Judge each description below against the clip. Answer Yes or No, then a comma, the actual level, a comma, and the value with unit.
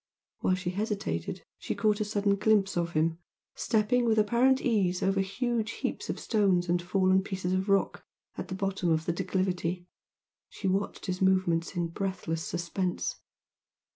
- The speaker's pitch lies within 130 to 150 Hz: No, high, 190 Hz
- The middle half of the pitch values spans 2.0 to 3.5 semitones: Yes, average, 2.8 semitones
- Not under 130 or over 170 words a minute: Yes, average, 160 wpm